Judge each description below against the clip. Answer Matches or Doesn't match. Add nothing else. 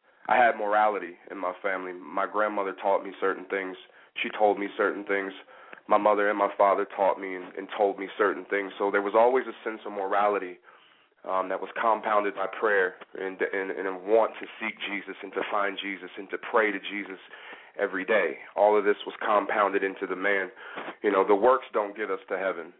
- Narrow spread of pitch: Matches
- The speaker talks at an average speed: Doesn't match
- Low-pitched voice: Matches